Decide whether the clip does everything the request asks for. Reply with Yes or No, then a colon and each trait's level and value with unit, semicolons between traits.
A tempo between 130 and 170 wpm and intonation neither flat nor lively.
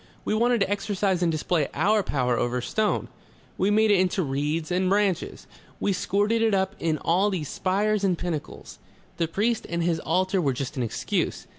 No: average, 185 wpm; average, 4.1 semitones